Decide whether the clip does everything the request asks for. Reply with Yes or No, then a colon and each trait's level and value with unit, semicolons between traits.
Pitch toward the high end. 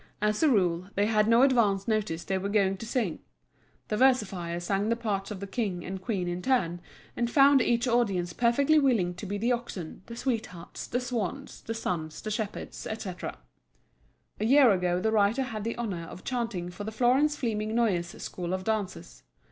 Yes: high, 215 Hz